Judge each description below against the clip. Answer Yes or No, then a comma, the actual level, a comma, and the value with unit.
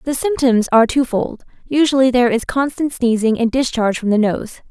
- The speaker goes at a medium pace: Yes, average, 180 wpm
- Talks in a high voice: Yes, high, 245 Hz